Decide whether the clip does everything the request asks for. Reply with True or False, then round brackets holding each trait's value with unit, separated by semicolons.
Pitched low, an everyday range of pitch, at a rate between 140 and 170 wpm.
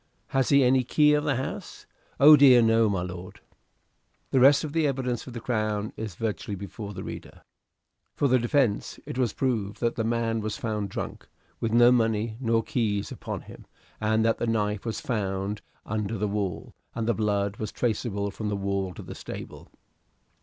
False (115 Hz; 3.2 semitones; 190 wpm)